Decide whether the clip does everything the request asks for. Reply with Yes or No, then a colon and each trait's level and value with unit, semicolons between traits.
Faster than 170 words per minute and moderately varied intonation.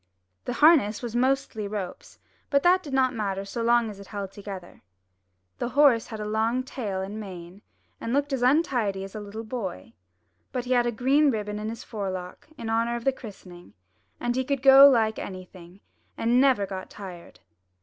Yes: average, 190 wpm; average, 4.4 semitones